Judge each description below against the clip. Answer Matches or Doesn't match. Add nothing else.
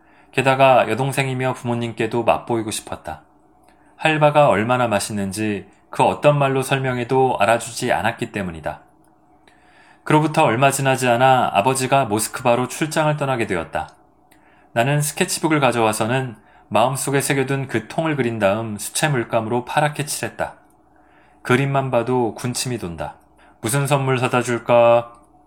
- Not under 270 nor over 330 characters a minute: Matches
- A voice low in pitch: Matches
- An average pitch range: Matches